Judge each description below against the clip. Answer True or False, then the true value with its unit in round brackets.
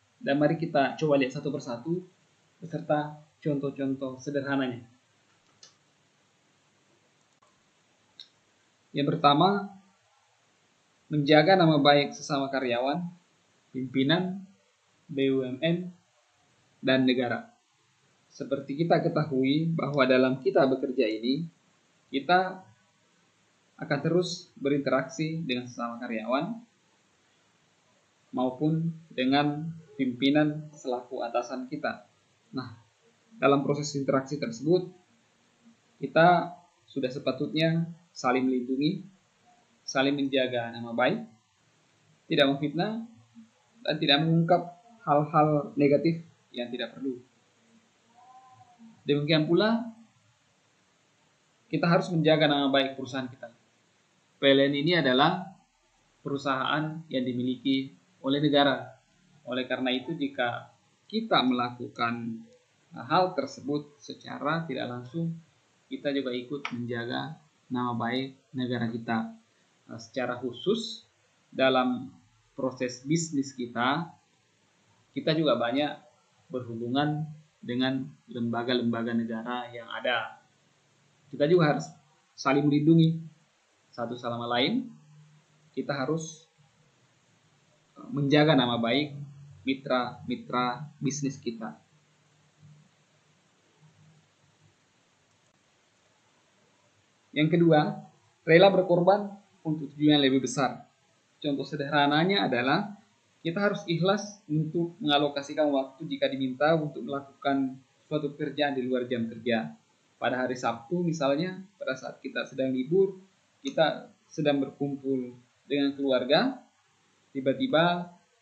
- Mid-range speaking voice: True (145 Hz)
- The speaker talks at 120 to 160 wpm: False (90 wpm)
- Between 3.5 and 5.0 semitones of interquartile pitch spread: True (3.9 semitones)